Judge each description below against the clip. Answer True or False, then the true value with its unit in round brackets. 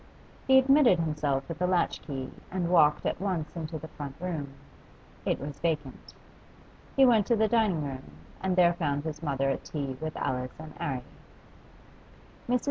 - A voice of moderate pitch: True (160 Hz)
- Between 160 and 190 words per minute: True (170 wpm)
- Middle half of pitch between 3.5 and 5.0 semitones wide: True (4.4 semitones)